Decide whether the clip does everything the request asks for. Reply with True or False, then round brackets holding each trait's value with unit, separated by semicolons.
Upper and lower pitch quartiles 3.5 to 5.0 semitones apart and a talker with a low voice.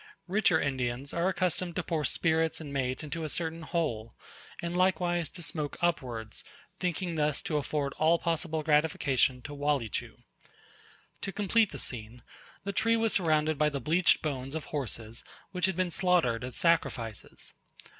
False (4.0 semitones; 155 Hz)